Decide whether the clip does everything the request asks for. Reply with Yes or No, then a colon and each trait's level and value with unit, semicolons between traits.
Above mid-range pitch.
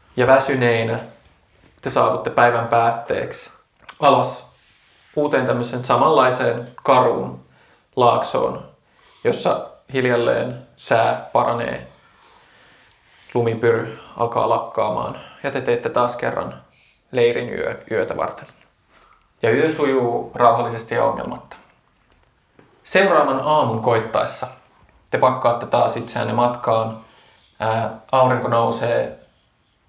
No: low, 115 Hz